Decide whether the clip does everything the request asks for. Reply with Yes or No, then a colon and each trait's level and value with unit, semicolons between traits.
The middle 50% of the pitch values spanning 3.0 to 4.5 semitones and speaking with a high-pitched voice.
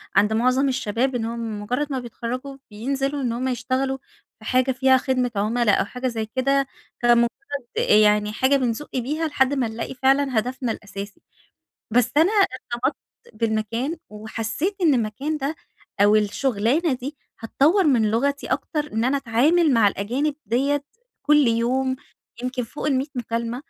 Yes: average, 3.4 semitones; very high, 255 Hz